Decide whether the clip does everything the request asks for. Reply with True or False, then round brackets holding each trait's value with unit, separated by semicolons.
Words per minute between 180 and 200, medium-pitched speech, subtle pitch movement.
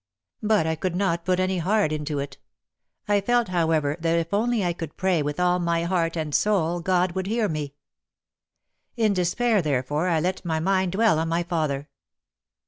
False (185 wpm; 175 Hz; 3.0 semitones)